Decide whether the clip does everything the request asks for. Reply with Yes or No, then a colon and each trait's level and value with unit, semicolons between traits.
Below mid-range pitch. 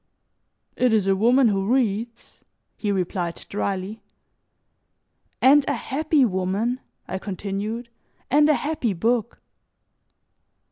No: high, 220 Hz